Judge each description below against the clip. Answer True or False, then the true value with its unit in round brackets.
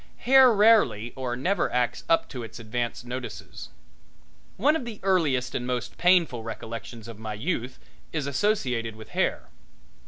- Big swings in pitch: True (8.0 semitones)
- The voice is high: False (125 Hz)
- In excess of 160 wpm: False (150 wpm)